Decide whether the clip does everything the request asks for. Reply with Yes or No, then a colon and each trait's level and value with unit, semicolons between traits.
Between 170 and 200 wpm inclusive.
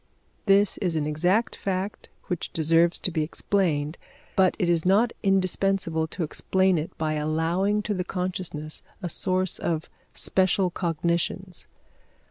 No: slow, 135 wpm